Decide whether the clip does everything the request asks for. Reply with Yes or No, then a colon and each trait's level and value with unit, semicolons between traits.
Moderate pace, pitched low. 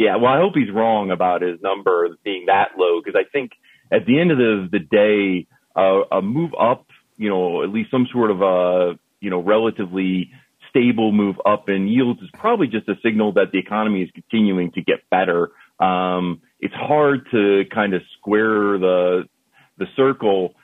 Yes: average, 190 wpm; low, 100 Hz